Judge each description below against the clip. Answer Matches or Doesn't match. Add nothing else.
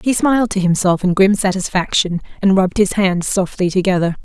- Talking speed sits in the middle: Matches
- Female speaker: Matches